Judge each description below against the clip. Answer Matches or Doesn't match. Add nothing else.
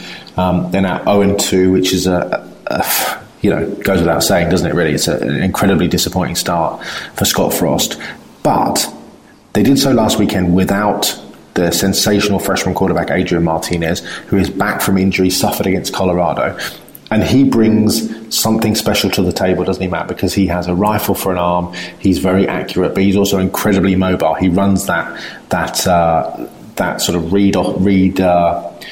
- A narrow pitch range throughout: Matches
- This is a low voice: Matches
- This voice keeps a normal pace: Matches